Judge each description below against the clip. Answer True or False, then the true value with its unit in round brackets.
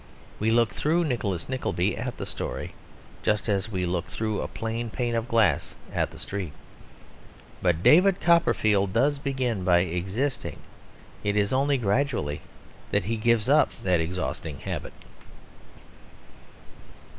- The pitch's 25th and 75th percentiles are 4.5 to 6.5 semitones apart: True (5.6 semitones)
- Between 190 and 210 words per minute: False (135 wpm)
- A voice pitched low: True (110 Hz)